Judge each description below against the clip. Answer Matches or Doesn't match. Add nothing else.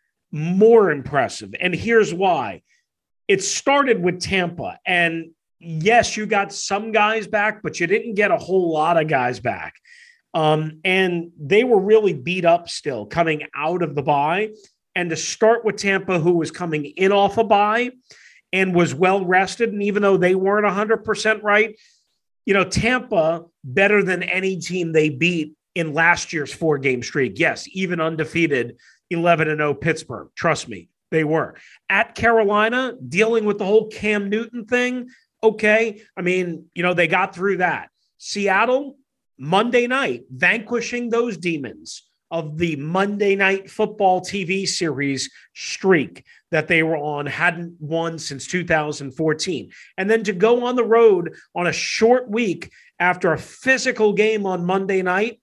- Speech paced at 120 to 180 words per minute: Matches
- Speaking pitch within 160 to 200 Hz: Matches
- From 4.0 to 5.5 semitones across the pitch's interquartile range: Matches